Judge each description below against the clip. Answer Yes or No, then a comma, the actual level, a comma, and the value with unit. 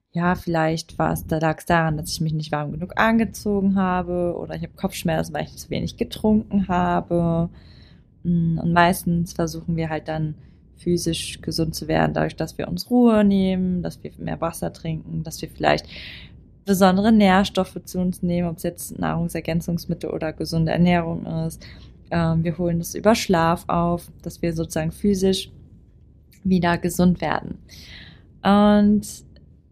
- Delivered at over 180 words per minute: No, average, 155 wpm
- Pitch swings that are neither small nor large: No, narrow, 2.3 semitones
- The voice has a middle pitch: Yes, medium, 170 Hz